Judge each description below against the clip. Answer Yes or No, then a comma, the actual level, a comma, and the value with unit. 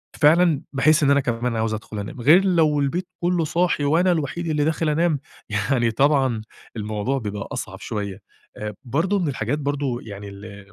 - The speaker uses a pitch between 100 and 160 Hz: Yes, medium, 140 Hz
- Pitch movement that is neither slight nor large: No, wide, 6.3 semitones